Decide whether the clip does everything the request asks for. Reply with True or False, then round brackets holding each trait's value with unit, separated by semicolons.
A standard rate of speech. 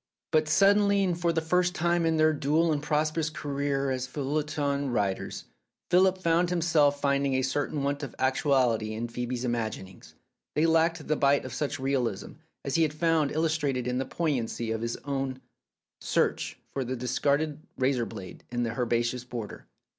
True (170 wpm)